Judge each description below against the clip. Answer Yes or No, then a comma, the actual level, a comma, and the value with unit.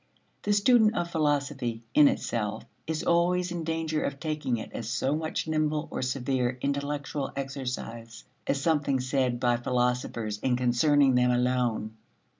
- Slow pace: No, average, 145 wpm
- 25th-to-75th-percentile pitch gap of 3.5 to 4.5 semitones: Yes, average, 3.8 semitones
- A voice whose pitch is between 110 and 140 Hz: Yes, low, 135 Hz